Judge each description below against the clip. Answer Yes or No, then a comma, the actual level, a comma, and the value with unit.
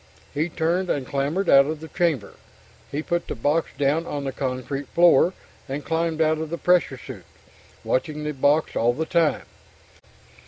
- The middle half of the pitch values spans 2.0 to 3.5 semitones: Yes, average, 3.1 semitones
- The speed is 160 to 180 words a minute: Yes, average, 170 wpm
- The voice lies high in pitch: No, medium, 150 Hz